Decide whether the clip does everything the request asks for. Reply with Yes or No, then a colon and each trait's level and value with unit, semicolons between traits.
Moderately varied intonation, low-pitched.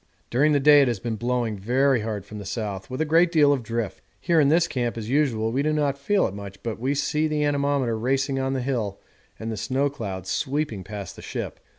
Yes: average, 4.6 semitones; low, 130 Hz